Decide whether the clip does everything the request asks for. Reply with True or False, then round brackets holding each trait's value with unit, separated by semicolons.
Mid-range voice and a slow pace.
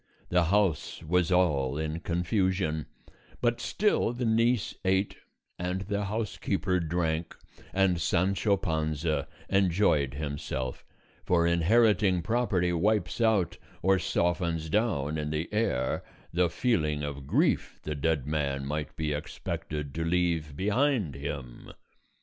False (85 Hz; 120 wpm)